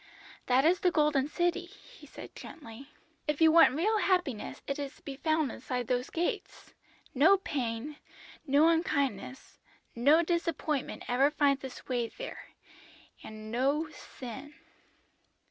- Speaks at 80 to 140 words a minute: Yes, slow, 135 wpm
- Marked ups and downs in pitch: No, average, 4.2 semitones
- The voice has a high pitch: Yes, very high, 285 Hz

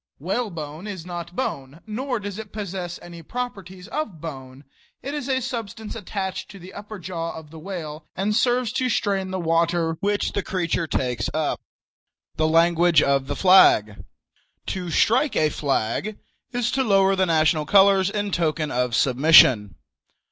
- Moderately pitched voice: Yes, medium, 180 Hz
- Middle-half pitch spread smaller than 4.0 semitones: No, average, 4.7 semitones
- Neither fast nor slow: Yes, average, 160 wpm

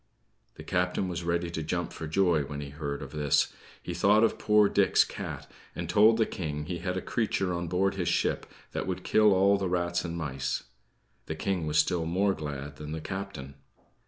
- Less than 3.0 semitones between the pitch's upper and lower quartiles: No, average, 3.9 semitones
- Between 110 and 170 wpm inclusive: No, fast, 205 wpm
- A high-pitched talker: No, very low, 85 Hz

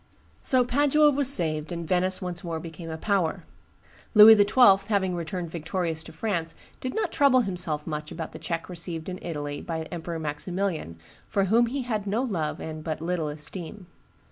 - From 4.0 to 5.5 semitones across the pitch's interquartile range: Yes, average, 4.4 semitones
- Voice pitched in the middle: Yes, medium, 175 Hz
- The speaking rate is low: No, average, 175 wpm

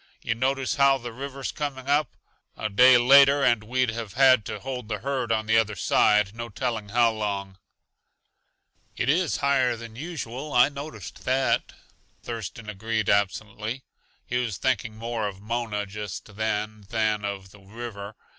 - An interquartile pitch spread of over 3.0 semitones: Yes, average, 3.6 semitones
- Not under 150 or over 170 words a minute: Yes, average, 160 wpm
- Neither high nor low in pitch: No, low, 115 Hz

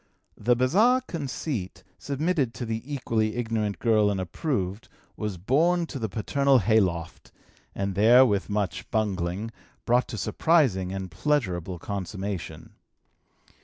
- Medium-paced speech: No, slow, 130 wpm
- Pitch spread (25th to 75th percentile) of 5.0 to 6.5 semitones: Yes, wide, 5.6 semitones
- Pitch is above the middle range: No, low, 110 Hz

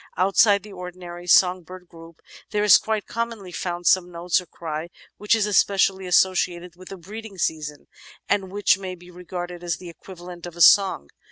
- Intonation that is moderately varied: No, narrow, 2.0 semitones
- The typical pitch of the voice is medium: Yes, medium, 180 Hz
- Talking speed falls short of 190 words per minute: Yes, average, 180 wpm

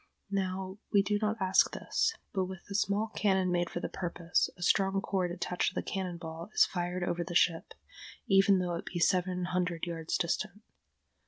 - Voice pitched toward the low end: No, medium, 185 Hz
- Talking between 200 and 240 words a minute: No, average, 190 wpm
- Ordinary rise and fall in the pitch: No, narrow, 1.9 semitones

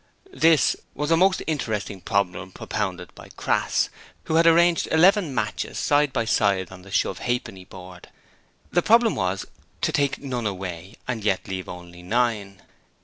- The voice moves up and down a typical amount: No, wide, 8.1 semitones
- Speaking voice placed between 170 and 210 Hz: No, low, 110 Hz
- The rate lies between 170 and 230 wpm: No, average, 155 wpm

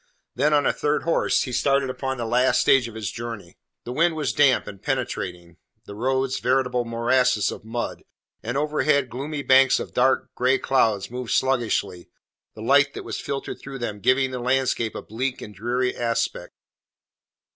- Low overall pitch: Yes, low, 125 Hz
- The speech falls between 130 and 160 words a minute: No, average, 175 wpm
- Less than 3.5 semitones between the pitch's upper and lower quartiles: Yes, narrow, 2.6 semitones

